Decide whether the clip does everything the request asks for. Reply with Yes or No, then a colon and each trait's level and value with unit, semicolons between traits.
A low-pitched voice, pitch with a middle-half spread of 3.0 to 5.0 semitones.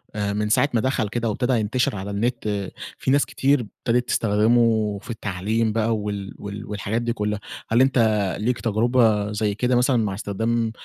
No: low, 110 Hz; narrow, 2.6 semitones